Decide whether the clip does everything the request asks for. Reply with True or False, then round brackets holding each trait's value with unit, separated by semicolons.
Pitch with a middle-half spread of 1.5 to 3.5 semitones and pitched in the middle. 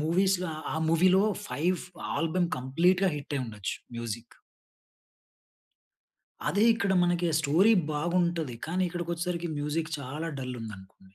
False (4.3 semitones; 165 Hz)